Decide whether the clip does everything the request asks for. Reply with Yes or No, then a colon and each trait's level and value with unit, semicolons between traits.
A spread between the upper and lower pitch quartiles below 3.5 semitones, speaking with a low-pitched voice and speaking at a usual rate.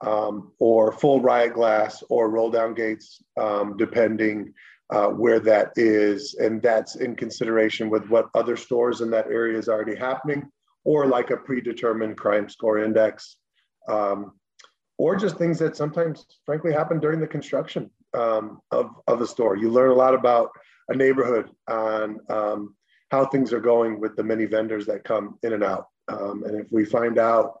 Yes: average, 3.0 semitones; low, 115 Hz; average, 175 wpm